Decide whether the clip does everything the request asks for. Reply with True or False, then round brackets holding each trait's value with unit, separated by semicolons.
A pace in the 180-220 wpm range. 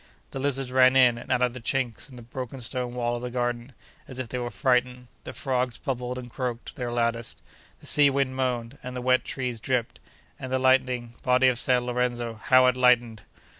True (205 wpm)